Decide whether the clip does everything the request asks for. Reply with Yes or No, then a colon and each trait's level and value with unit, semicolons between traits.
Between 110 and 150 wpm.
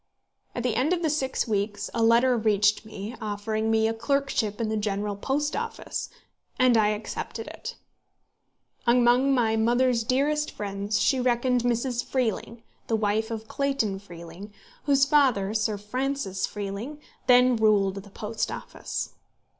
Yes: average, 145 wpm